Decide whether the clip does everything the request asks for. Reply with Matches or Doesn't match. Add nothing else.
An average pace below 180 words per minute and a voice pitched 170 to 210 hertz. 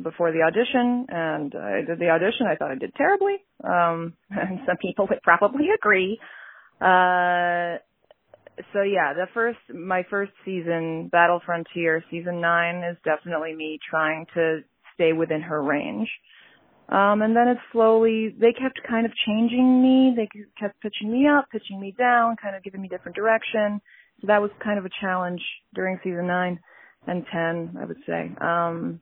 Matches